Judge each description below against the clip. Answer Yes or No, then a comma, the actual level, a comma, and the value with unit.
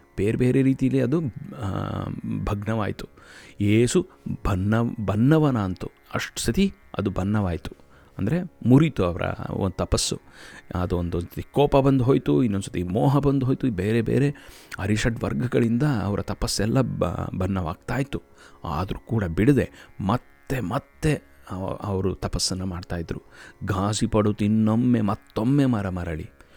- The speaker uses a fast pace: Yes, fast, 115 wpm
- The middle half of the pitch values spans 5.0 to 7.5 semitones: Yes, average, 5.3 semitones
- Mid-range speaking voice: No, low, 105 Hz